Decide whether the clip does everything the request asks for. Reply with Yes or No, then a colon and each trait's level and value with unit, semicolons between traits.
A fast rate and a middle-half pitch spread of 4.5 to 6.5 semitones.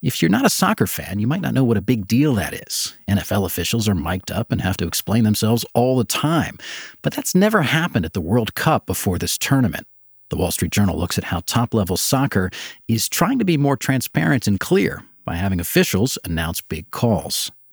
Yes: fast, 215 wpm; wide, 5.6 semitones